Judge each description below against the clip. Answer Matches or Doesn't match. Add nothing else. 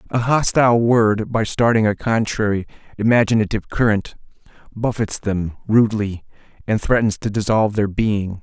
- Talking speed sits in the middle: Doesn't match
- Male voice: Matches